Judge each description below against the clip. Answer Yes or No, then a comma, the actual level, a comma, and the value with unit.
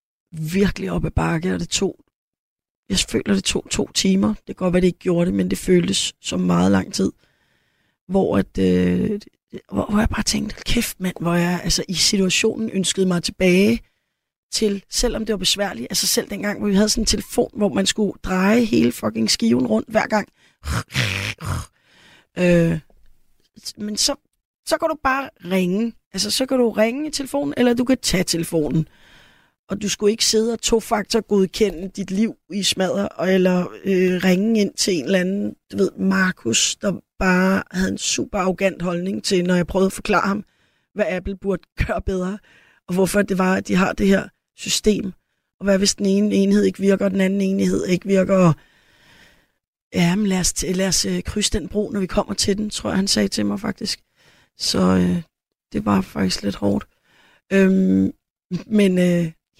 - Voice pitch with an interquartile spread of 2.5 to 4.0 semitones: Yes, average, 2.8 semitones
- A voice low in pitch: No, high, 195 Hz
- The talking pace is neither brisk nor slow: Yes, average, 190 wpm